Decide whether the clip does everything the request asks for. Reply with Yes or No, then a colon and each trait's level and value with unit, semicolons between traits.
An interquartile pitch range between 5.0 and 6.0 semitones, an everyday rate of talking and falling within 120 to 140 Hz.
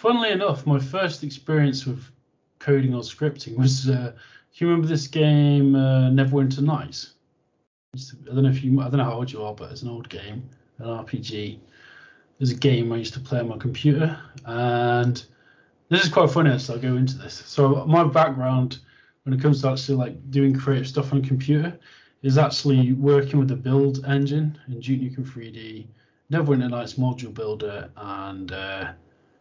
No: average, 2.8 semitones; average, 180 wpm; low, 130 Hz